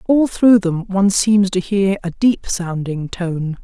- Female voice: Yes, female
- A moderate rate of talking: Yes, average, 180 wpm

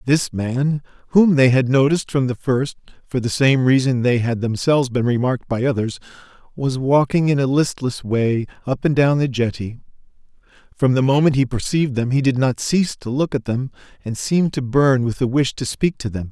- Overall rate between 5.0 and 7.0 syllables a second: Yes, 5.3 syllables/s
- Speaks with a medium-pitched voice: No, low, 130 Hz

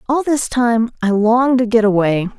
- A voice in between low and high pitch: No, high, 230 Hz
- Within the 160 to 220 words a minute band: Yes, average, 200 wpm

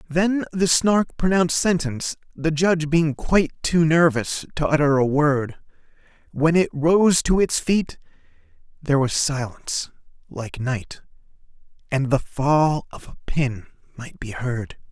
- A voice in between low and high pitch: Yes, medium, 150 Hz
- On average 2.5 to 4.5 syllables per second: Yes, 4.2 syllables/s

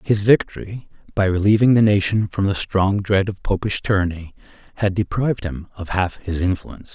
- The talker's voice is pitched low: Yes, low, 100 Hz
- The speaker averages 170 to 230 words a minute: Yes, average, 175 wpm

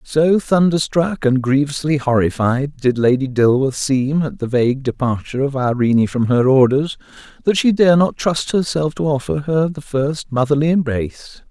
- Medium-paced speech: Yes, average, 160 wpm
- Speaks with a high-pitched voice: No, medium, 140 Hz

